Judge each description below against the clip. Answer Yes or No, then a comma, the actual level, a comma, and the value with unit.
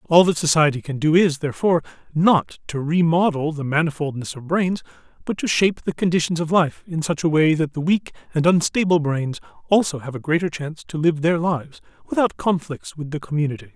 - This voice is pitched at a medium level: Yes, medium, 160 Hz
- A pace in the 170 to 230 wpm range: Yes, average, 195 wpm